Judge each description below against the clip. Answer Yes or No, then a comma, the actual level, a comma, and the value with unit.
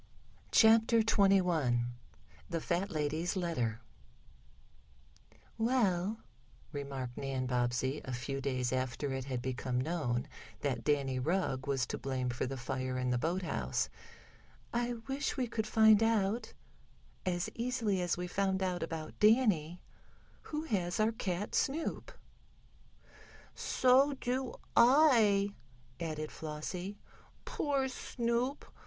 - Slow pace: Yes, slow, 115 wpm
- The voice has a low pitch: No, medium, 175 Hz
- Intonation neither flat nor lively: No, wide, 8.8 semitones